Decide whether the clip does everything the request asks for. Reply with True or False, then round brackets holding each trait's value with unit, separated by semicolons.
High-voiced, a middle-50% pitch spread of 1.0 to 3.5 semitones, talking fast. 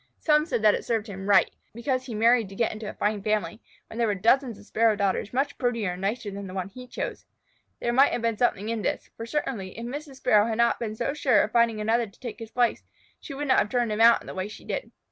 True (230 Hz; 2.9 semitones; 275 wpm)